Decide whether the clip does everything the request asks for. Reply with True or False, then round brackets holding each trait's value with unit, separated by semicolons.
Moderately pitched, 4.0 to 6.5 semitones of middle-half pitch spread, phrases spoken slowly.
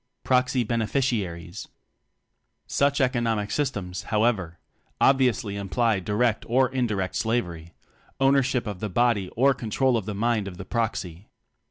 False (115 Hz; 4.3 semitones; 125 wpm)